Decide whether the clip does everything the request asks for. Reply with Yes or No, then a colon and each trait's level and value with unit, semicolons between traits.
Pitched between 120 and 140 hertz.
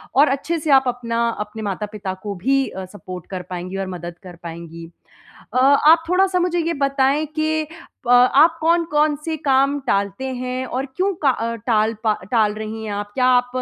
No: very high, 250 Hz